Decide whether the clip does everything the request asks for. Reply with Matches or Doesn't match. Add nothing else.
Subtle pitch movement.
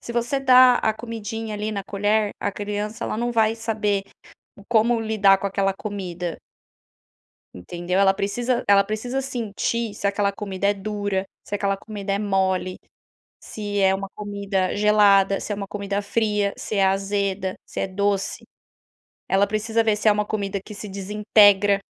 Matches